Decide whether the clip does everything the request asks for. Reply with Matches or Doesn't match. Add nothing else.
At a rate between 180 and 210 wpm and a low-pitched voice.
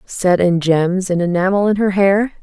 Doesn't match